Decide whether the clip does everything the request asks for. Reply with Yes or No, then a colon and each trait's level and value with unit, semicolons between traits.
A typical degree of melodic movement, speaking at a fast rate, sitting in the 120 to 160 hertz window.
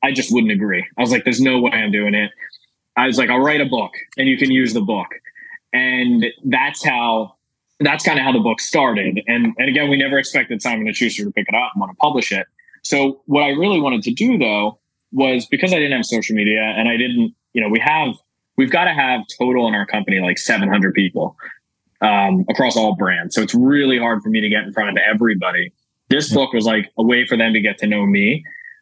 Yes: average, 5.0 semitones; fast, 235 wpm; low, 125 Hz